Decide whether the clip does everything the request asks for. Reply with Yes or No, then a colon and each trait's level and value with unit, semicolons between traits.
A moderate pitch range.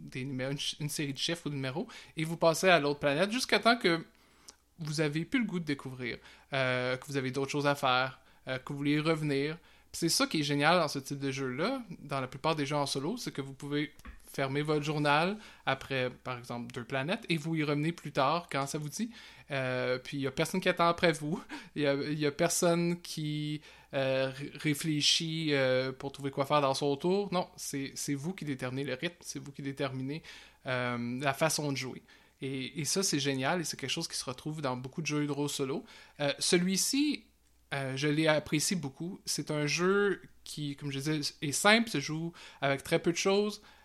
Yes: average, 3.6 semitones